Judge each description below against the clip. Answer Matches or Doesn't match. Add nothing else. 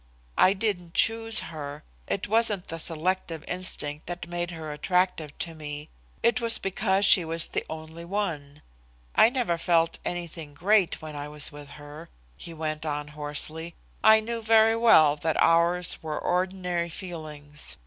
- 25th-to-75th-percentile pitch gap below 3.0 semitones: Doesn't match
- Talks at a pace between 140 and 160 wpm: Matches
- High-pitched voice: Doesn't match